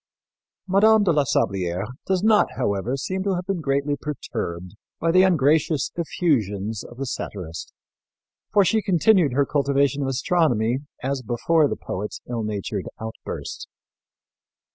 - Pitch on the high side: No, medium, 140 Hz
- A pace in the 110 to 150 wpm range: Yes, average, 140 wpm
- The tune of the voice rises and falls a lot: Yes, wide, 7.8 semitones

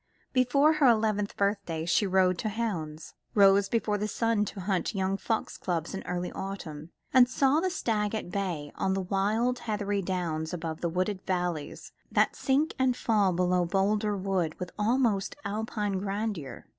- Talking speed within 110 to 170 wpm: Yes, average, 165 wpm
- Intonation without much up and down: No, average, 3.4 semitones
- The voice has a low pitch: No, high, 200 Hz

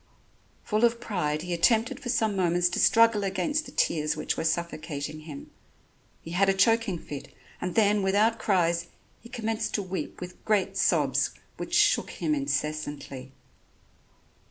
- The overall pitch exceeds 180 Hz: Yes, high, 190 Hz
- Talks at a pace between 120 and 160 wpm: Yes, average, 155 wpm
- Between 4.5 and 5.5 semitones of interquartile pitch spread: Yes, average, 5.2 semitones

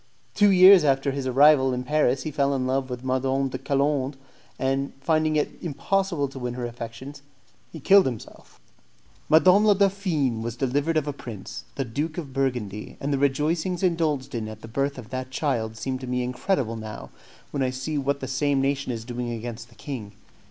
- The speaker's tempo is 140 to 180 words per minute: No, average, 195 wpm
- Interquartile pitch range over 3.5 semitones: No, average, 3.1 semitones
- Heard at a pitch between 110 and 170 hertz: Yes, low, 135 Hz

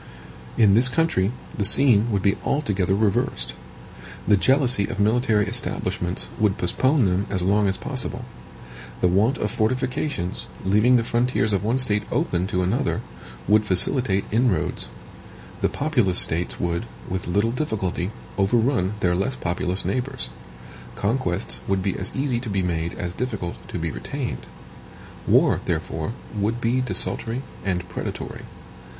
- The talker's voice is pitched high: No, low, 105 Hz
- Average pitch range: Yes, average, 4.9 semitones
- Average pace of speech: Yes, average, 145 wpm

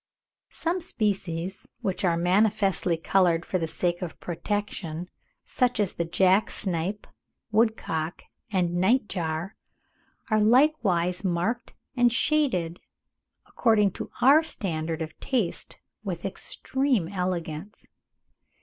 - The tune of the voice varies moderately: Yes, average, 4.3 semitones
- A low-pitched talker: No, high, 190 Hz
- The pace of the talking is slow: Yes, slow, 110 wpm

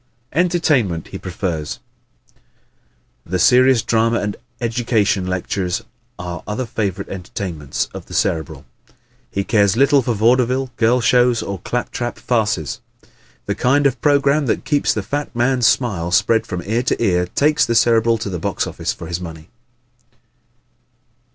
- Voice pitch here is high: No, low, 110 Hz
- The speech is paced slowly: No, average, 150 wpm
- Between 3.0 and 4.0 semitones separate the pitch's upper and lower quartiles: No, average, 5.3 semitones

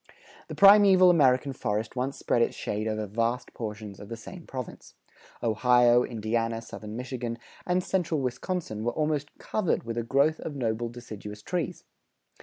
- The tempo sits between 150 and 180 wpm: Yes, average, 155 wpm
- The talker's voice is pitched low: Yes, low, 120 Hz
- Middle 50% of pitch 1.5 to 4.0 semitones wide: No, average, 5.0 semitones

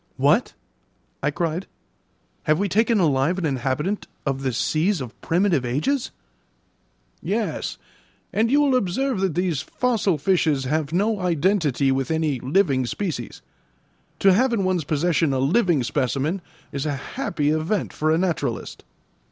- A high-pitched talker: No, medium, 165 Hz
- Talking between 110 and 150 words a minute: Yes, average, 145 wpm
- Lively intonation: Yes, wide, 5.8 semitones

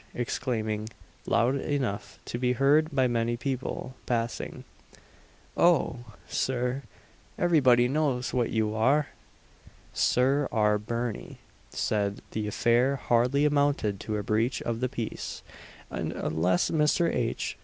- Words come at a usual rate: No, slow, 120 wpm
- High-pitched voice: No, low, 120 Hz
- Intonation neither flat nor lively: Yes, average, 3.6 semitones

